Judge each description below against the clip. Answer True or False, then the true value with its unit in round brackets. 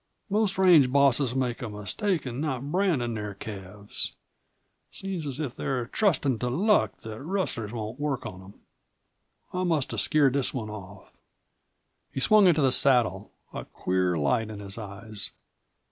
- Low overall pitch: True (125 Hz)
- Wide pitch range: True (6.2 semitones)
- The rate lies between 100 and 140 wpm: False (160 wpm)